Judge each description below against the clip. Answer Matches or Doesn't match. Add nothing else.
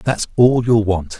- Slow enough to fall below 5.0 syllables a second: Matches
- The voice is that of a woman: Doesn't match